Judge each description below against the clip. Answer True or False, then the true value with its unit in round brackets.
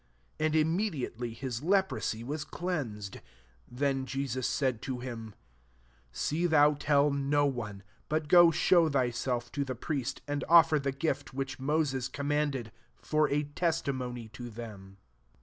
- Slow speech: False (150 wpm)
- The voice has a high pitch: False (140 Hz)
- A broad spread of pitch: False (3.9 semitones)